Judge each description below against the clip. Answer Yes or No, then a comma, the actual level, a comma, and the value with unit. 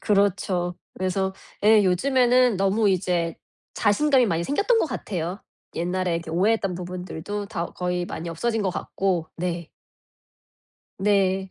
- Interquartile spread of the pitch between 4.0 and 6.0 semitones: No, average, 3.0 semitones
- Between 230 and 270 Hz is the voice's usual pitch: No, high, 190 Hz